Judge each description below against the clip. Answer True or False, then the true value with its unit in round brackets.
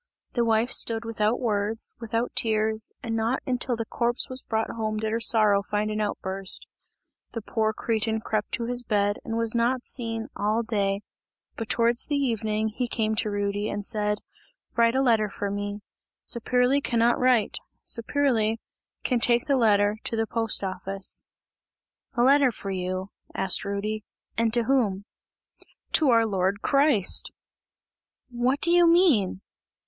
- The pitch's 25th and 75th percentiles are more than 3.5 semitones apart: False (2.5 semitones)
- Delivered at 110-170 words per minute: True (155 wpm)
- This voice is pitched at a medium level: False (225 Hz)